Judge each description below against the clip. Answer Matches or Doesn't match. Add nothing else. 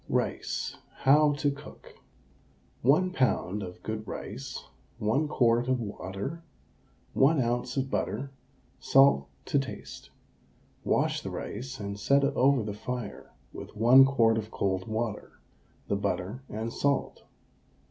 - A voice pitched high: Doesn't match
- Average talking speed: Doesn't match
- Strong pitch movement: Doesn't match